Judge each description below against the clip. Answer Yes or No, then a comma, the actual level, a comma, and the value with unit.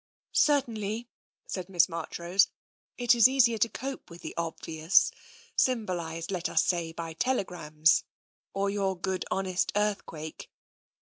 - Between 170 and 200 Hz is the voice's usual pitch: Yes, high, 190 Hz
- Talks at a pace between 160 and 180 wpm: No, average, 140 wpm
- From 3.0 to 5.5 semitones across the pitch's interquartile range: Yes, average, 4.7 semitones